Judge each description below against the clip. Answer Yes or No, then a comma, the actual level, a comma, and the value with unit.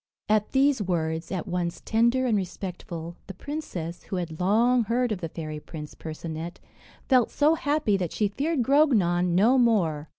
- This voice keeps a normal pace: Yes, average, 165 wpm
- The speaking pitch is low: No, high, 195 Hz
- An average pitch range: No, wide, 6.3 semitones